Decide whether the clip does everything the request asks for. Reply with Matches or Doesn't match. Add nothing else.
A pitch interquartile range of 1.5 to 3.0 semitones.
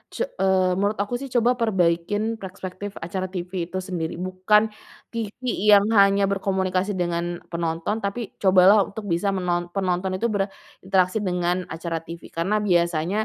Matches